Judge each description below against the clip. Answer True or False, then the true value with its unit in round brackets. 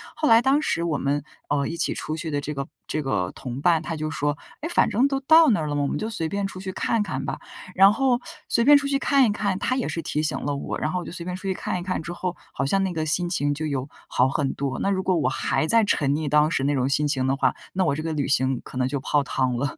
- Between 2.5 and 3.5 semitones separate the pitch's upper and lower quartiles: False (5.6 semitones)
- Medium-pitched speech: True (160 Hz)